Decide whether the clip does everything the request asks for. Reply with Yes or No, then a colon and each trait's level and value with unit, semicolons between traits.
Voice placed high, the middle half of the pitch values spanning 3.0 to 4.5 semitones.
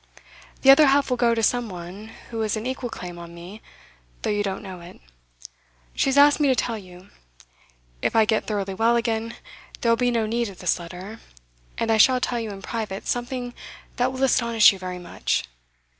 Yes: high, 225 Hz; average, 4.0 semitones